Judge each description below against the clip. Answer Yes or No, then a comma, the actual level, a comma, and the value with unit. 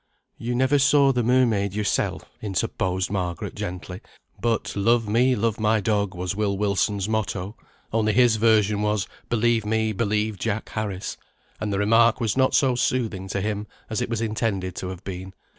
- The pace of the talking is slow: No, average, 170 wpm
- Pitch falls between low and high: No, low, 105 Hz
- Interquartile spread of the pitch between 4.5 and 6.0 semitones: No, average, 2.7 semitones